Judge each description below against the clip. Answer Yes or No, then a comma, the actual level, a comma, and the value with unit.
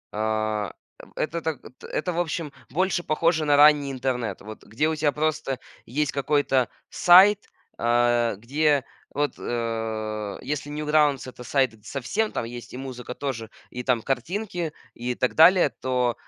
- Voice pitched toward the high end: No, low, 135 Hz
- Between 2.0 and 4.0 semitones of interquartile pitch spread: No, average, 4.5 semitones